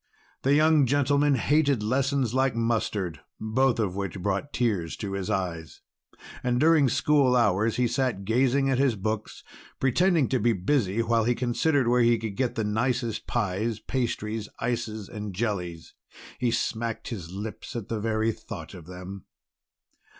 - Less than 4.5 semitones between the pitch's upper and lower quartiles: Yes, average, 4.1 semitones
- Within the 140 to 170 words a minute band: Yes, average, 155 wpm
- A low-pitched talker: Yes, low, 115 Hz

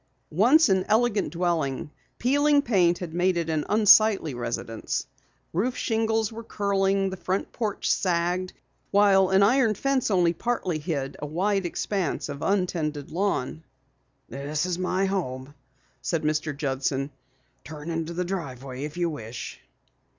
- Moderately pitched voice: Yes, medium, 180 Hz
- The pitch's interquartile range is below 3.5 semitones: No, average, 4.9 semitones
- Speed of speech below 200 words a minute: Yes, average, 140 wpm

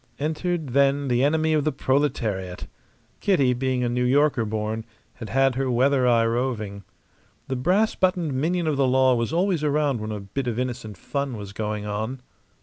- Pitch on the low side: Yes, low, 130 Hz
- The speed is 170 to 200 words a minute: Yes, average, 180 wpm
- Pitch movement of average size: Yes, average, 4.2 semitones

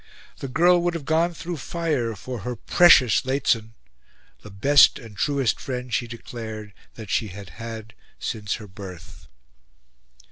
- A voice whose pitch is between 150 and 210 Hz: No, low, 115 Hz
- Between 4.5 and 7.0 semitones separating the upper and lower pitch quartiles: Yes, average, 5.0 semitones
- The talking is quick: No, average, 145 wpm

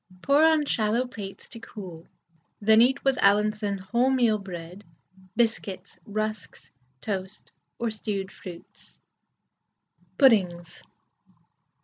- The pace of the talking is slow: Yes, slow, 95 wpm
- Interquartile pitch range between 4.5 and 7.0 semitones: No, average, 3.5 semitones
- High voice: Yes, high, 215 Hz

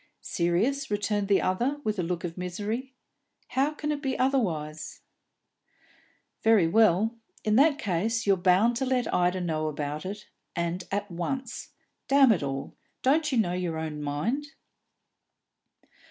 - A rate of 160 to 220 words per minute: No, average, 145 wpm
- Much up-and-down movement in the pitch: Yes, wide, 7.0 semitones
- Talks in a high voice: Yes, high, 205 Hz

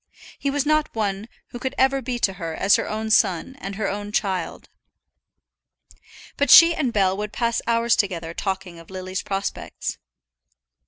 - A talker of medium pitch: No, high, 205 Hz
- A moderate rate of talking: Yes, average, 165 wpm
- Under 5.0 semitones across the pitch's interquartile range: Yes, average, 4.2 semitones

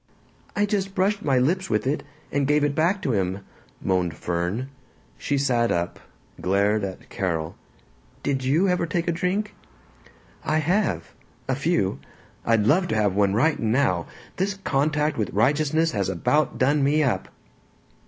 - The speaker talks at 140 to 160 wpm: Yes, average, 155 wpm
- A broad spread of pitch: Yes, wide, 8.0 semitones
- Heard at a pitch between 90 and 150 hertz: Yes, medium, 140 Hz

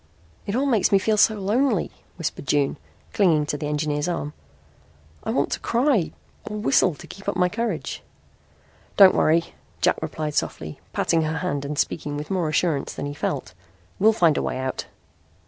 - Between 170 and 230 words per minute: Yes, average, 180 wpm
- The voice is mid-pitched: Yes, medium, 165 Hz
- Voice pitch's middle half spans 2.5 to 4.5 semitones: No, wide, 5.4 semitones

